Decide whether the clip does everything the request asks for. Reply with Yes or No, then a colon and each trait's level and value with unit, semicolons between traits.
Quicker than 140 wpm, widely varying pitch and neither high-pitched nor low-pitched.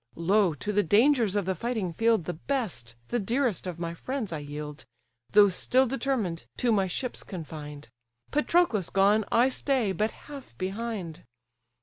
No: average, 155 wpm; wide, 6.2 semitones; high, 205 Hz